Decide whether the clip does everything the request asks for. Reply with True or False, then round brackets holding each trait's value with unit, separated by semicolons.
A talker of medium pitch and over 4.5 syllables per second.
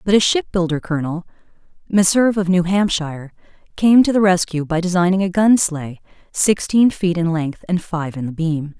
True (180 Hz; 5.2 syllables/s)